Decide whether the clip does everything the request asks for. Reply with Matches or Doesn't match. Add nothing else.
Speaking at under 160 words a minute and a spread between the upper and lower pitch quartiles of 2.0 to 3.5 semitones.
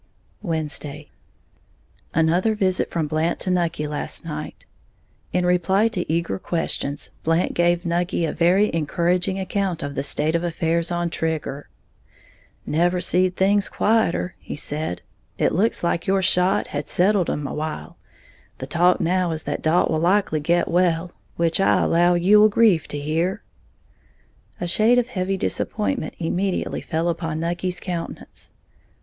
Matches